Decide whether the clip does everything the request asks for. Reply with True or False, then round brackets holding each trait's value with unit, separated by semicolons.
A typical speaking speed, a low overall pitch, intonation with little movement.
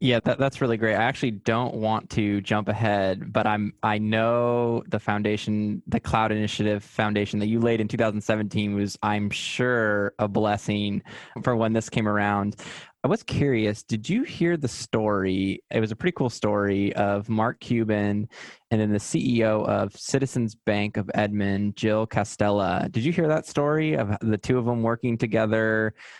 True (175 wpm; 110 Hz; 2.1 semitones)